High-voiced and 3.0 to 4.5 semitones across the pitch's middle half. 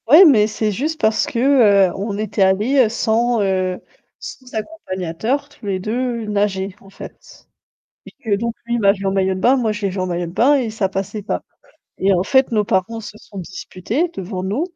Yes: high, 210 Hz; average, 3.7 semitones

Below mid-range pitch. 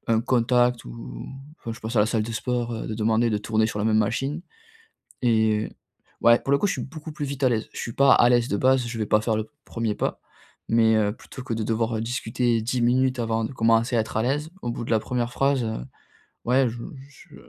Yes: low, 115 Hz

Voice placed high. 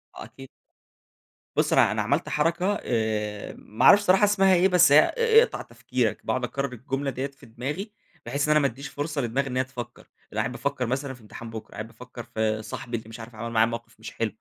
No: low, 130 Hz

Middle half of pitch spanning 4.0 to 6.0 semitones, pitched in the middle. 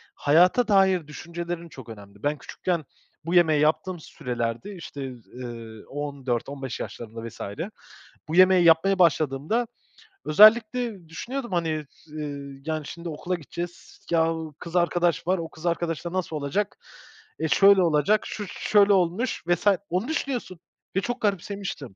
Yes: average, 4.4 semitones; medium, 165 Hz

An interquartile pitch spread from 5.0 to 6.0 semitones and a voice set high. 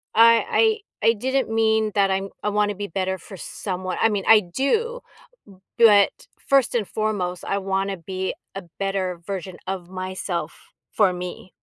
No: average, 2.9 semitones; high, 195 Hz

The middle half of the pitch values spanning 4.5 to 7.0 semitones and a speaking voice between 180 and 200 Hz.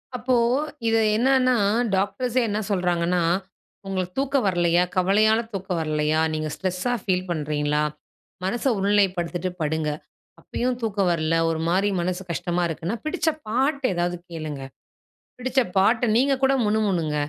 Yes: average, 5.1 semitones; medium, 185 Hz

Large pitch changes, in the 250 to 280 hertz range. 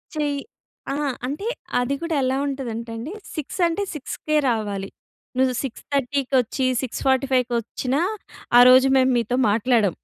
No: average, 2.9 semitones; very high, 260 Hz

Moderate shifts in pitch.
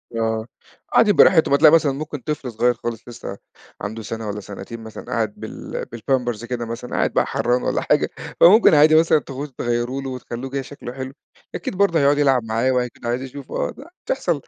Yes: average, 3.6 semitones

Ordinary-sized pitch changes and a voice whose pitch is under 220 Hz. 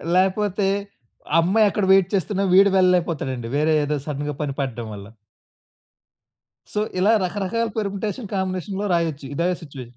Yes: average, 5.0 semitones; medium, 185 Hz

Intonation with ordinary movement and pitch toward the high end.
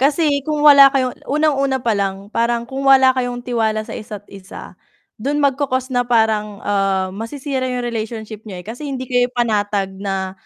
Yes: average, 4.1 semitones; high, 240 Hz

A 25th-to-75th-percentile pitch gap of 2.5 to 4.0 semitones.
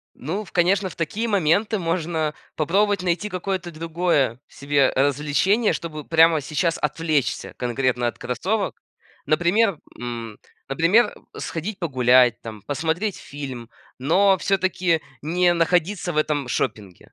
No: average, 5.0 semitones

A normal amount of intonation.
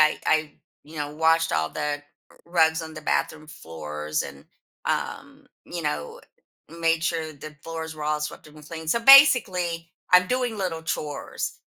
No: narrow, 1.8 semitones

